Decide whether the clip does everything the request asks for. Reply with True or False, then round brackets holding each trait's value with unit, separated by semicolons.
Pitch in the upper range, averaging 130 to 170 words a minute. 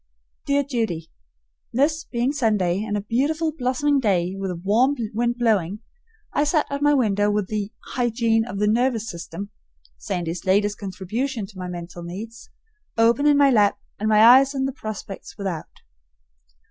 True (220 Hz; 160 wpm)